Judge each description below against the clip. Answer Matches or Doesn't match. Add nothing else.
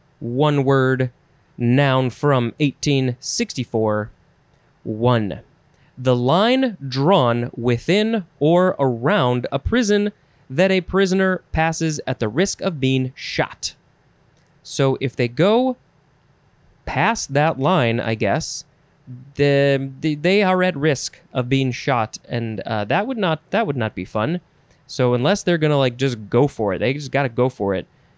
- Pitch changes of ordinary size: Matches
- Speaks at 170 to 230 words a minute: Doesn't match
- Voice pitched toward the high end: Doesn't match